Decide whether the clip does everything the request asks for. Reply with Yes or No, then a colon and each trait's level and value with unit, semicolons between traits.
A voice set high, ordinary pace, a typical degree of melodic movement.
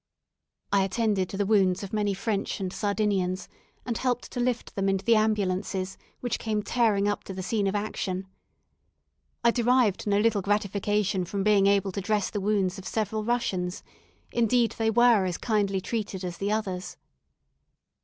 No: high, 205 Hz; average, 170 wpm; narrow, 2.3 semitones